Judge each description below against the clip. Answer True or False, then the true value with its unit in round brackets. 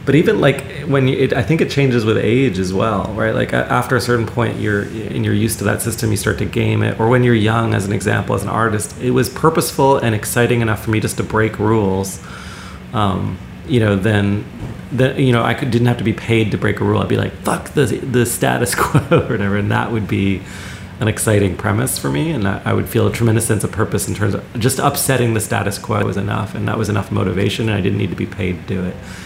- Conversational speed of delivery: False (255 wpm)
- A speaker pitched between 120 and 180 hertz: False (110 Hz)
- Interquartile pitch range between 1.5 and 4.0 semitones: True (3.1 semitones)